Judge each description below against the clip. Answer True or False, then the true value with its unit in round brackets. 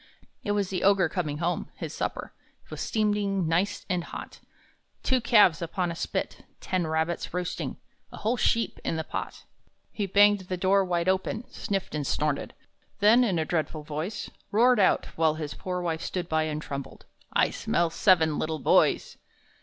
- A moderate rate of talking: True (170 wpm)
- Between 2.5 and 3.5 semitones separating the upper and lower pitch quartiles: False (4.0 semitones)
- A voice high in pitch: False (180 Hz)